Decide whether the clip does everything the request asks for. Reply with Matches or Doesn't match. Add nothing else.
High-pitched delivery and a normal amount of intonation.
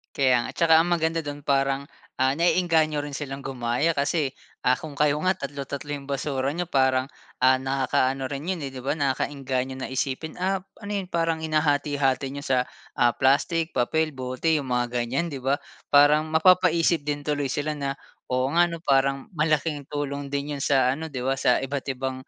Doesn't match